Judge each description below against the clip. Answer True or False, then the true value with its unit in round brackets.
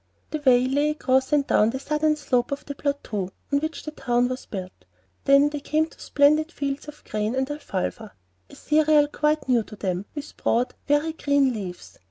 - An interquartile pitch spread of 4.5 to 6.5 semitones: False (3.5 semitones)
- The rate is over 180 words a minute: True (195 wpm)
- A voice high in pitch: True (280 Hz)